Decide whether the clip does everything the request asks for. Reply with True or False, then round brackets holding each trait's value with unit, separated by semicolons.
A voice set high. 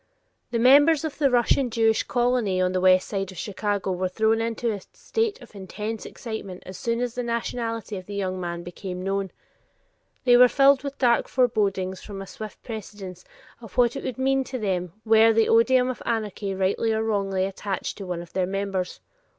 True (215 Hz)